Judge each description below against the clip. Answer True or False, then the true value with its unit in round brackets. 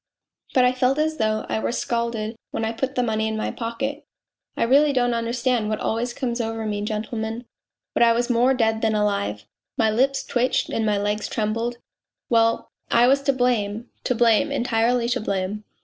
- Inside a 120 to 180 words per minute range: False (190 wpm)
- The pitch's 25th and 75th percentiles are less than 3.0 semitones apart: True (2.5 semitones)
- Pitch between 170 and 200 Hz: False (230 Hz)